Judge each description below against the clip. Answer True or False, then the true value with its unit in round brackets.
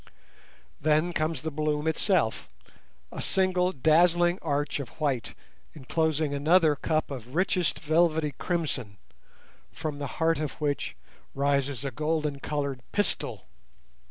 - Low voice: False (155 Hz)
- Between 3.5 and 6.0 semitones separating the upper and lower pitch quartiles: False (2.6 semitones)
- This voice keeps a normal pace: False (120 wpm)